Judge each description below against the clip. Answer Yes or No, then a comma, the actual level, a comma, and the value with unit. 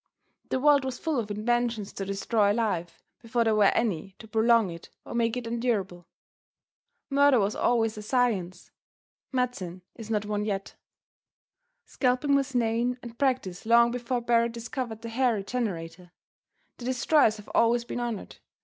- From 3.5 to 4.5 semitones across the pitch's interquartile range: No, average, 3.0 semitones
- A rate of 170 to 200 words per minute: No, average, 155 wpm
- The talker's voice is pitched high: Yes, high, 230 Hz